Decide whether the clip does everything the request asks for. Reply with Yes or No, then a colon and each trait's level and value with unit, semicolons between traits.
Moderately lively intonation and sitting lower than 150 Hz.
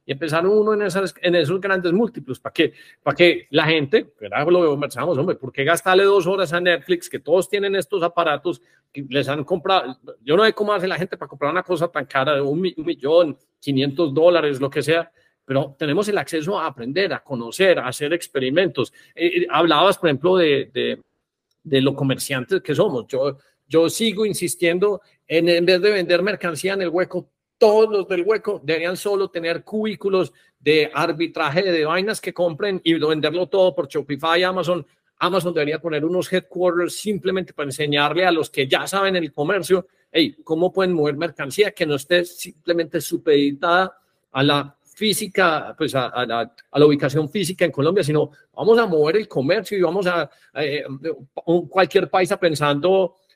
No: average, 4.0 semitones; medium, 175 Hz